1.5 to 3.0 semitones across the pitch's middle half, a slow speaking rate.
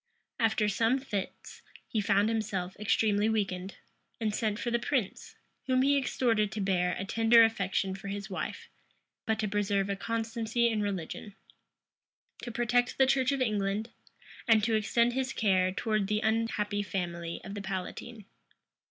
No: narrow, 2.6 semitones; average, 155 wpm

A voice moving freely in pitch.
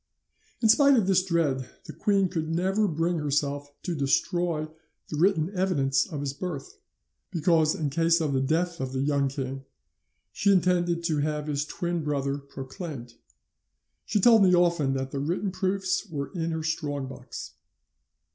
No: average, 4.2 semitones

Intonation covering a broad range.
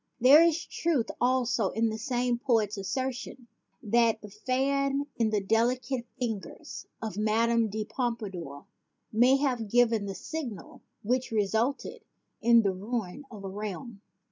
No: average, 3.2 semitones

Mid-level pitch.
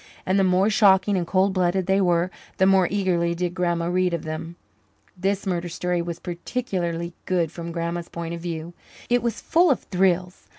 Yes: medium, 180 Hz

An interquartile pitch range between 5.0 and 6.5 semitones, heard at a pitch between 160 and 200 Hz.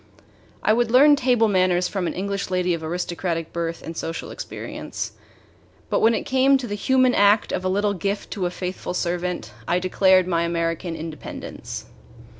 No: average, 3.4 semitones; medium, 185 Hz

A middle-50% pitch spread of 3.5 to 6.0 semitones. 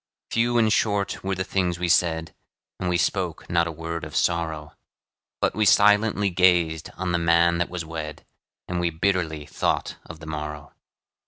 No: narrow, 2.5 semitones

